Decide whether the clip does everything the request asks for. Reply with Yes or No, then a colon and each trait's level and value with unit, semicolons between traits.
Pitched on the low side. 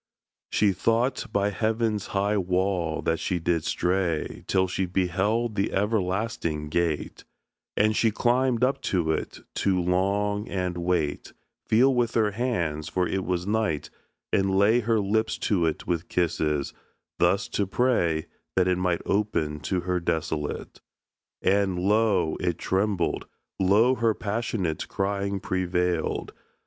Yes: very low, 95 Hz